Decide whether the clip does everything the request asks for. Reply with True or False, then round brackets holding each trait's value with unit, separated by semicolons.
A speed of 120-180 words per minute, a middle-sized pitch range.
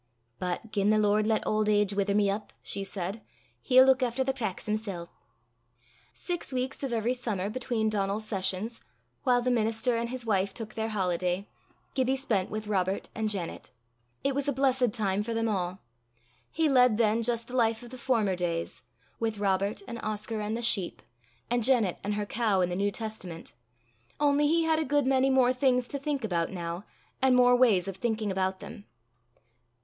False (190 wpm; 4.0 semitones)